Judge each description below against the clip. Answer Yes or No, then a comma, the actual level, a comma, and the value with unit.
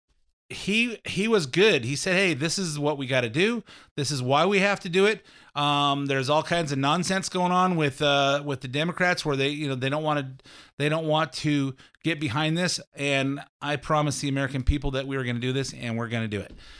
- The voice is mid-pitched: Yes, medium, 145 Hz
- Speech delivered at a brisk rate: Yes, fast, 245 wpm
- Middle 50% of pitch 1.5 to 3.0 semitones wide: No, average, 4.0 semitones